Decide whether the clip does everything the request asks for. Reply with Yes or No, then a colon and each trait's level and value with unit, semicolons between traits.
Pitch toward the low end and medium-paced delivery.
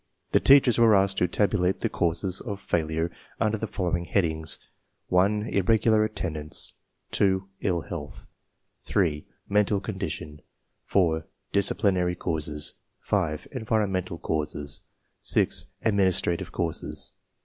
No: very low, 95 Hz; slow, 110 wpm